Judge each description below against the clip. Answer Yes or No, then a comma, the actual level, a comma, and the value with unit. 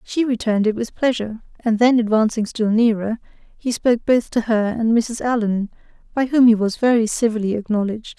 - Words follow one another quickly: No, average, 185 wpm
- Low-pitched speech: No, high, 225 Hz